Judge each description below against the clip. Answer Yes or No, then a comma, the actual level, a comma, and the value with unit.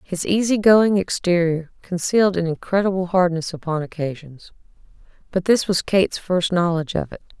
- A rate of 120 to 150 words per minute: Yes, average, 145 wpm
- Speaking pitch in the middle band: Yes, medium, 180 Hz